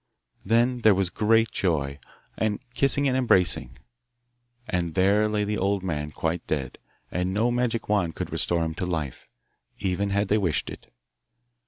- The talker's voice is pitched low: Yes, very low, 95 Hz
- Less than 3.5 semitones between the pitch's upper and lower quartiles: No, average, 4.4 semitones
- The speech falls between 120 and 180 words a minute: Yes, average, 160 wpm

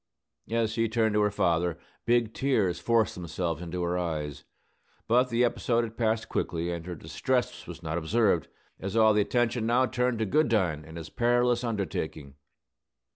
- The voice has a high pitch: No, low, 110 Hz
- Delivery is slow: No, average, 165 wpm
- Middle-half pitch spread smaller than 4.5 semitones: No, average, 5.3 semitones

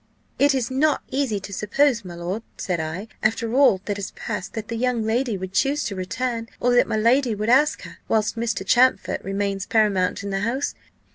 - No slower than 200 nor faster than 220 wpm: Yes, fast, 205 wpm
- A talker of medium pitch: No, high, 220 Hz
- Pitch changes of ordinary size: Yes, average, 4.2 semitones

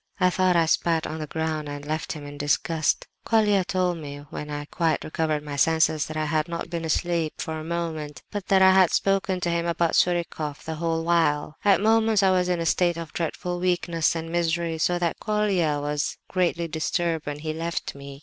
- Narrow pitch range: Yes, narrow, 2.3 semitones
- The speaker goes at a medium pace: No, fast, 210 wpm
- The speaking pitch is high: No, medium, 165 Hz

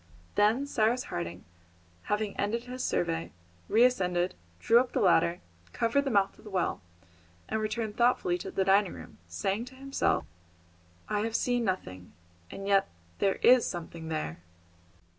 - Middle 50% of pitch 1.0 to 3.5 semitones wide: No, average, 5.0 semitones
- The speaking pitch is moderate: No, high, 205 Hz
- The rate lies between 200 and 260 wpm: No, average, 155 wpm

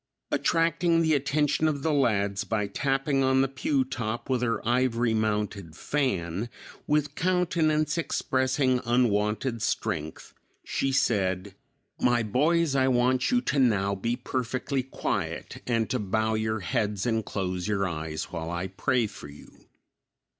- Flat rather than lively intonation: No, average, 4.8 semitones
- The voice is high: No, low, 120 Hz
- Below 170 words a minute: Yes, average, 140 wpm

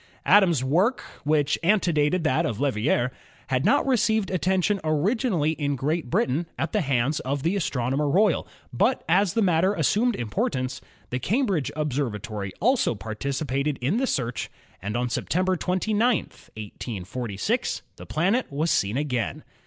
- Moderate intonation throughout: No, wide, 6.9 semitones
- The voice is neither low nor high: Yes, medium, 150 Hz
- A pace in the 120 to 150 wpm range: Yes, average, 145 wpm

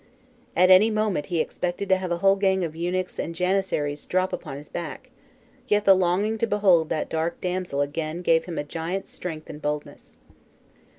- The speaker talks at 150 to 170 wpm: No, average, 185 wpm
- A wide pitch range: No, average, 3.0 semitones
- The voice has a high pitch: No, medium, 180 Hz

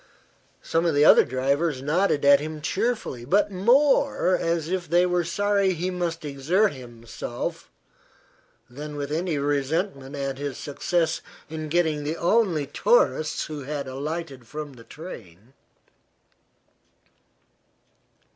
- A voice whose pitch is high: No, medium, 155 Hz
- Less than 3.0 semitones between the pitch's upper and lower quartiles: No, average, 4.0 semitones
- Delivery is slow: Yes, slow, 125 wpm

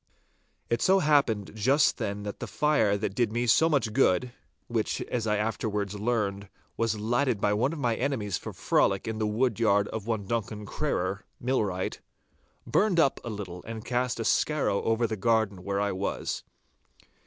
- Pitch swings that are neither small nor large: Yes, average, 3.1 semitones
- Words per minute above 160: Yes, average, 170 wpm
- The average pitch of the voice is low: Yes, low, 110 Hz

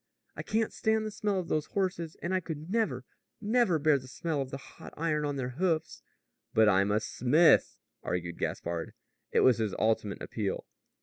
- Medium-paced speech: Yes, average, 185 wpm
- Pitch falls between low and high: Yes, medium, 150 Hz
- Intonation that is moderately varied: No, wide, 8.1 semitones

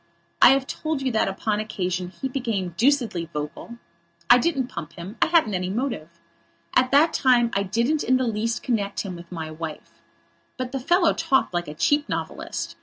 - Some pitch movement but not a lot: No, wide, 6.6 semitones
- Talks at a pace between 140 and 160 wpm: No, average, 190 wpm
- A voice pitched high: Yes, high, 230 Hz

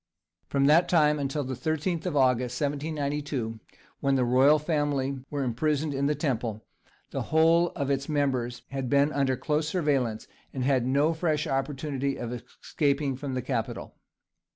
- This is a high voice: No, medium, 140 Hz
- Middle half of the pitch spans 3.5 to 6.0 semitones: No, narrow, 2.5 semitones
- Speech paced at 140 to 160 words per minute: Yes, average, 155 wpm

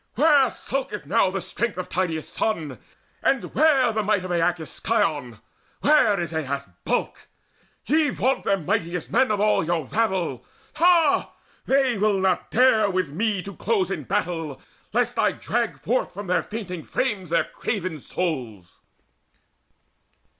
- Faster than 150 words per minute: No, average, 145 wpm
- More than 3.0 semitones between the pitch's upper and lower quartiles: Yes, wide, 5.6 semitones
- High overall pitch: Yes, high, 195 Hz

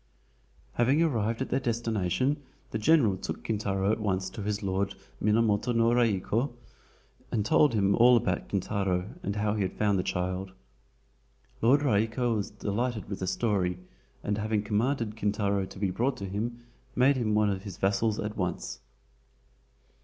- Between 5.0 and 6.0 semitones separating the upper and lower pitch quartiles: No, average, 3.1 semitones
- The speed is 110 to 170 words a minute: Yes, average, 160 wpm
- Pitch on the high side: No, low, 105 Hz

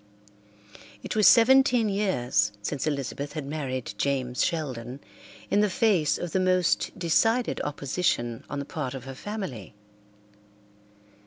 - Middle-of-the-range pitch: Yes, medium, 150 Hz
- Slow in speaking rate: Yes, slow, 130 wpm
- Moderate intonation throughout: No, wide, 7.0 semitones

